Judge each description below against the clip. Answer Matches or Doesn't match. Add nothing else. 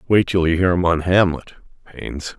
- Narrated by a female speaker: Doesn't match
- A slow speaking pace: Doesn't match